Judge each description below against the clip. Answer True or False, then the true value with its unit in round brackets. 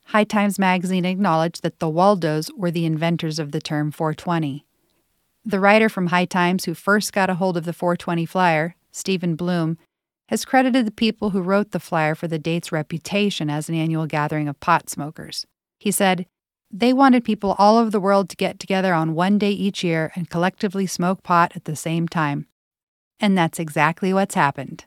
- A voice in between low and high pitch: True (175 Hz)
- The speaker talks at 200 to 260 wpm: False (190 wpm)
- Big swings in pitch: False (3.5 semitones)